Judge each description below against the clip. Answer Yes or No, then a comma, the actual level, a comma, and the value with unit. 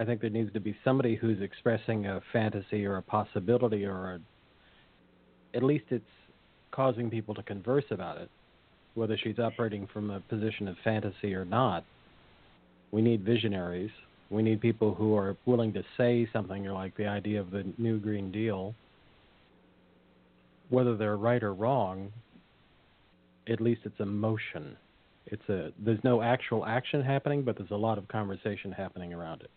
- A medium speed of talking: Yes, average, 165 wpm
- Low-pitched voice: Yes, low, 105 Hz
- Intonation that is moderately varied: Yes, average, 3.0 semitones